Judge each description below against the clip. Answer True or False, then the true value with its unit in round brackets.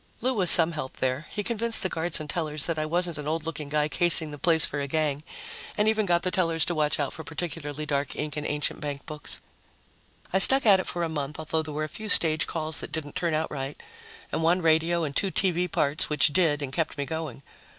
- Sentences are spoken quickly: True (240 wpm)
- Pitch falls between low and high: True (160 Hz)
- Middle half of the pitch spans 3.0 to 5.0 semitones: False (2.6 semitones)